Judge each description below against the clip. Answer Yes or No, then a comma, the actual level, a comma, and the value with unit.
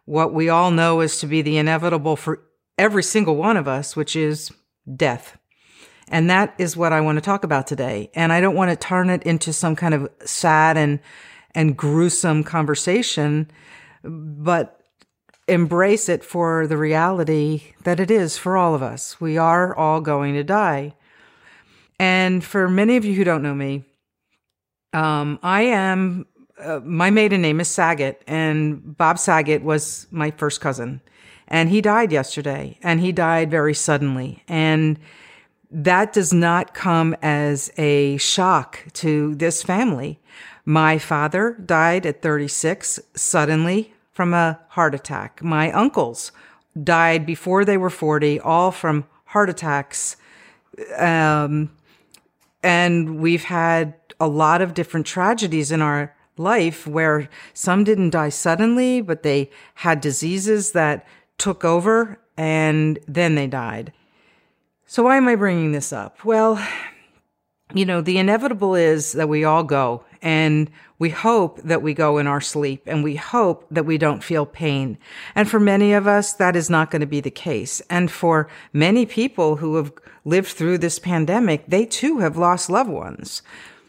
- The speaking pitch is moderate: Yes, medium, 165 Hz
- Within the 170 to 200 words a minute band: No, average, 155 wpm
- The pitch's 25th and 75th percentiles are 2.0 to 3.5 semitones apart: Yes, average, 3.2 semitones